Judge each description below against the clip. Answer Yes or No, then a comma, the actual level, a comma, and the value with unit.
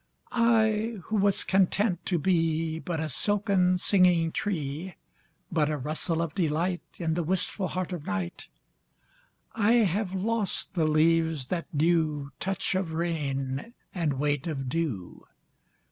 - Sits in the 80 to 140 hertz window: No, medium, 170 Hz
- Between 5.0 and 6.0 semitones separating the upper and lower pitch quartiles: No, average, 3.7 semitones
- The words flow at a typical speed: No, slow, 115 wpm